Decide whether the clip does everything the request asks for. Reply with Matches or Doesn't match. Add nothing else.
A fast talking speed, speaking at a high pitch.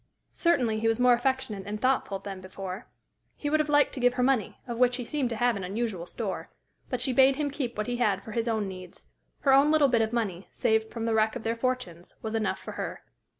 Matches